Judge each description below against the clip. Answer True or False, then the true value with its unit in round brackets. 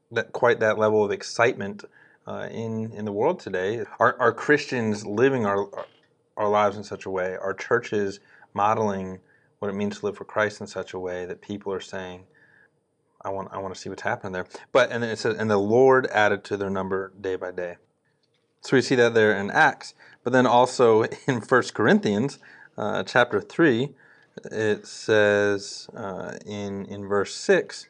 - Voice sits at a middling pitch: False (105 Hz)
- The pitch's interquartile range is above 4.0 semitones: False (2.9 semitones)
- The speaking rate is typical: True (190 wpm)